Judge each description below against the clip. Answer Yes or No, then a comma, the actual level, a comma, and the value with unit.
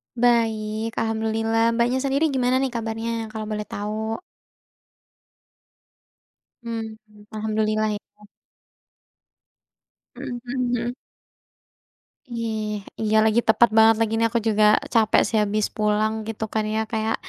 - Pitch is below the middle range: No, high, 225 Hz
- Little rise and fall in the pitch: Yes, narrow, 1.4 semitones